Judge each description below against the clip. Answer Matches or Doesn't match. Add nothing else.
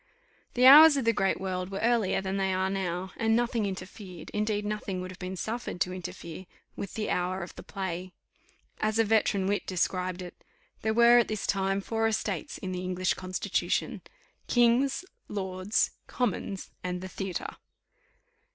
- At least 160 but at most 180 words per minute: Matches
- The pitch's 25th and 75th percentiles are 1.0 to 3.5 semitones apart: Matches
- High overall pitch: Matches